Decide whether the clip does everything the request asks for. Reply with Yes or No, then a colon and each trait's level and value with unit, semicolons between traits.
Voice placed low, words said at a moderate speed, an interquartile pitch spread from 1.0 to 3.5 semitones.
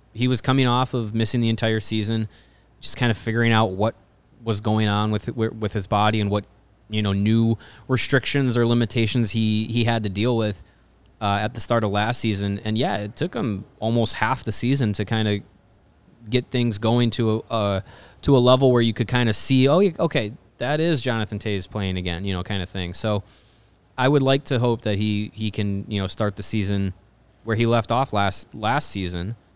No: low, 110 Hz; fast, 215 wpm; narrow, 2.5 semitones